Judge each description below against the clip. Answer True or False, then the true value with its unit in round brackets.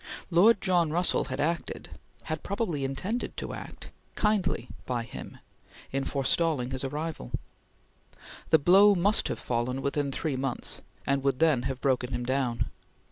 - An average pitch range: True (4.8 semitones)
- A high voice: False (140 Hz)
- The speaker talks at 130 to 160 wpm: True (145 wpm)